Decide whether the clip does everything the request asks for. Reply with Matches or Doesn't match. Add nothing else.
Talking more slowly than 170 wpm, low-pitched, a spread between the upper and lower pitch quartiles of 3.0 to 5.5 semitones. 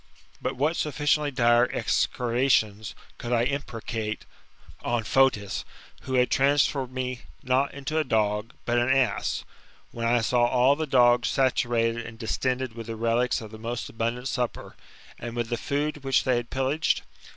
Doesn't match